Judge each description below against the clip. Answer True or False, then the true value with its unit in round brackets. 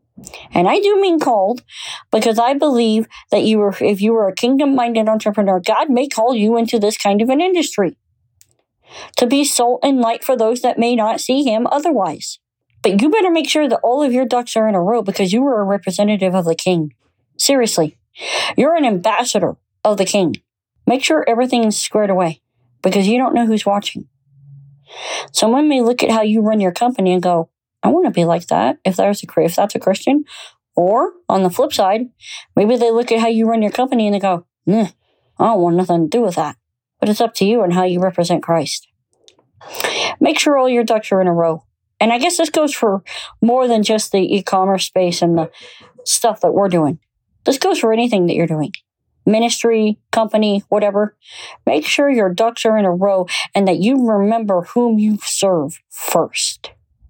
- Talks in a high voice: True (215 Hz)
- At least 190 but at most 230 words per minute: True (205 wpm)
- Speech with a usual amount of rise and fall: True (4.6 semitones)